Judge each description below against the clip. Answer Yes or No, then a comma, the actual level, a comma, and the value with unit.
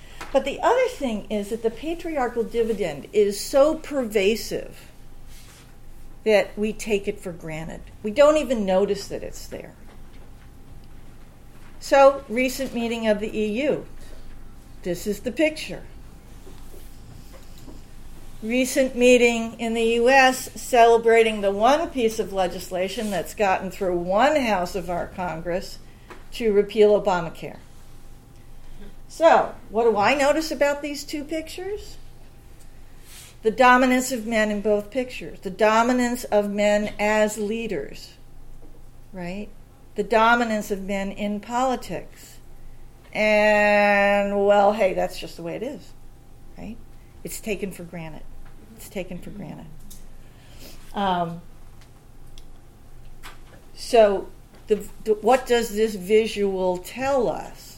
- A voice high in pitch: Yes, high, 210 Hz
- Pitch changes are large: No, average, 4.2 semitones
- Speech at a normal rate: No, slow, 120 wpm